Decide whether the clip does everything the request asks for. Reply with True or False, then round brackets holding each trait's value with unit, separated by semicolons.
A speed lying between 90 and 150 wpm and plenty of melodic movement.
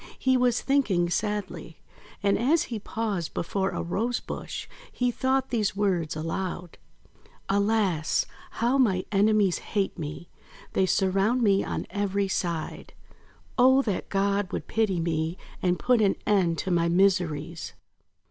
False (140 wpm; 4.1 semitones)